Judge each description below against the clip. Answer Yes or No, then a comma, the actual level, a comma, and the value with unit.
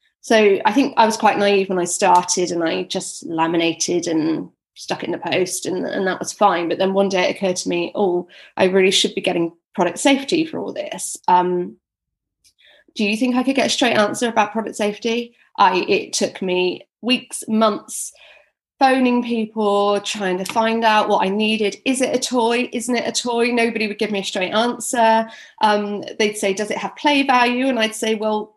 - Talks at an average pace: No, fast, 210 wpm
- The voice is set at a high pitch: Yes, high, 215 Hz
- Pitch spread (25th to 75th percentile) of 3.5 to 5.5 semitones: Yes, average, 4.0 semitones